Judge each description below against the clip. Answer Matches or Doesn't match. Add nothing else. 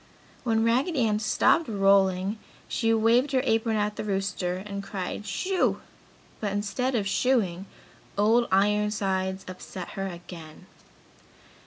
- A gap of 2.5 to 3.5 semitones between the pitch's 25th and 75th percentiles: Matches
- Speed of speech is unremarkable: Doesn't match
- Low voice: Doesn't match